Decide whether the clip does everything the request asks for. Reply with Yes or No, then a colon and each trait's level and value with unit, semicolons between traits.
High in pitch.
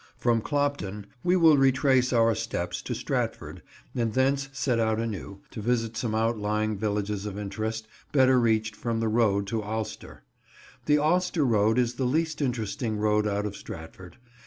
No: low, 115 Hz